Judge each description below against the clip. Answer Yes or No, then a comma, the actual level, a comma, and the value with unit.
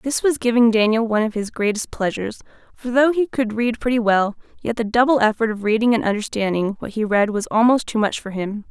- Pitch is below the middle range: No, high, 225 Hz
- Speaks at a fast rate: Yes, fast, 225 wpm